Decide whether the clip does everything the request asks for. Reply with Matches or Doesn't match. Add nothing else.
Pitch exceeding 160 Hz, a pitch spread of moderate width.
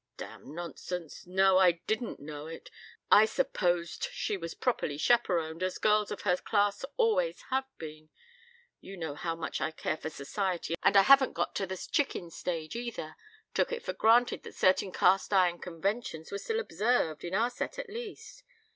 Doesn't match